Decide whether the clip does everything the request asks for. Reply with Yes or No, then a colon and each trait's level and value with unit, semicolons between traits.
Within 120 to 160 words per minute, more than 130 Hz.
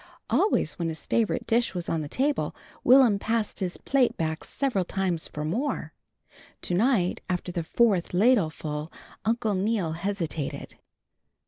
Yes: average, 140 wpm; high, 190 Hz